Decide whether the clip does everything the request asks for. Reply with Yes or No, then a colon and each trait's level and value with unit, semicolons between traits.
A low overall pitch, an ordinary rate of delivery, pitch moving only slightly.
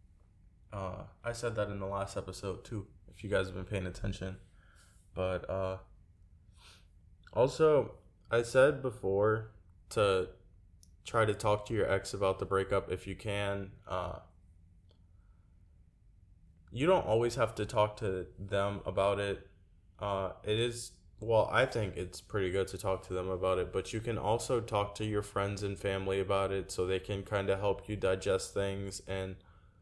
Yes: very low, 95 Hz; average, 165 wpm; narrow, 2.1 semitones